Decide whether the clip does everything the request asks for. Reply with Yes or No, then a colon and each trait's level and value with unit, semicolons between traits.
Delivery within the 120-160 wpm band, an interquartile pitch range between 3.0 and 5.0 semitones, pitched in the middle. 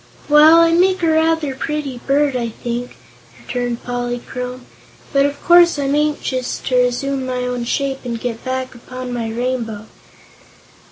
No: average, 150 wpm; average, 3.3 semitones; very high, 255 Hz